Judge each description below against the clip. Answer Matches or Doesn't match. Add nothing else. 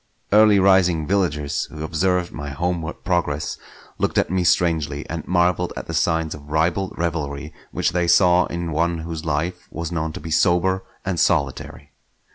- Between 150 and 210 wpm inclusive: Matches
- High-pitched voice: Doesn't match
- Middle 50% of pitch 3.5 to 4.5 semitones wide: Doesn't match